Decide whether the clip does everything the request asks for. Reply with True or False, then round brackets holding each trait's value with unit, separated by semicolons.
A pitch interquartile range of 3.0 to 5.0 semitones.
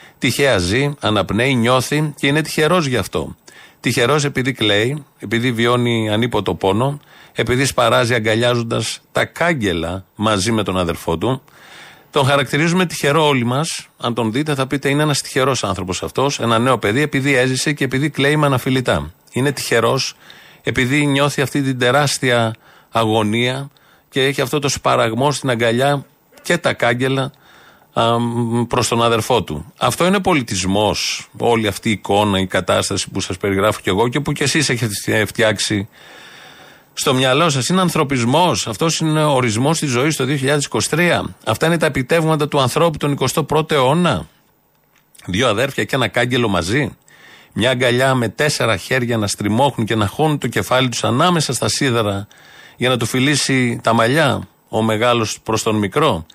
True (4.5 semitones)